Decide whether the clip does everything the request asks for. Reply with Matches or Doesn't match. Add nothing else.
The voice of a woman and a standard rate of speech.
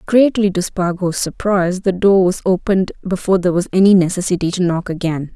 Matches